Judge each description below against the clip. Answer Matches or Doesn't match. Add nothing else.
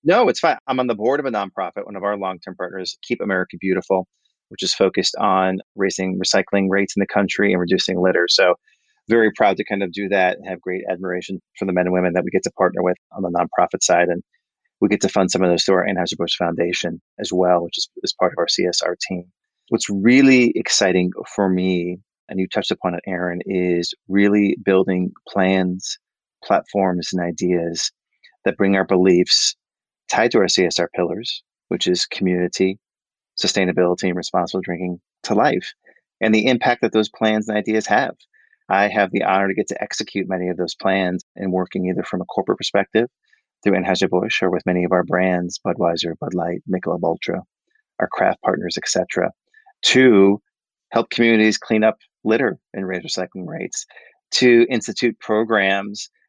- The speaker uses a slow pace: Doesn't match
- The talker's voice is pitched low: Matches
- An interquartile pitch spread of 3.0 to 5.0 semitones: Doesn't match